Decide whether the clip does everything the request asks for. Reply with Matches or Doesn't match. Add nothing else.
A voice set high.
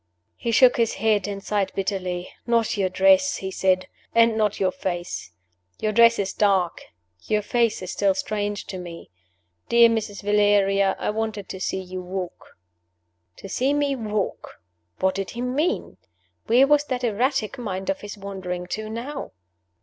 Matches